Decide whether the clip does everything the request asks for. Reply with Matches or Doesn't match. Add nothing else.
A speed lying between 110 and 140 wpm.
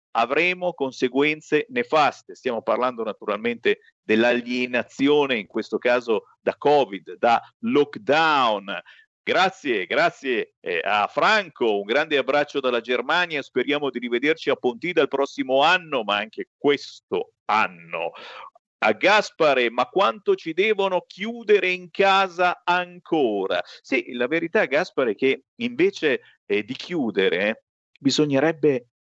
Matches